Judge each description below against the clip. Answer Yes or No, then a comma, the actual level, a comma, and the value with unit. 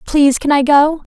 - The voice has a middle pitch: No, very high, 290 Hz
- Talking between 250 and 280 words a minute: No, average, 200 wpm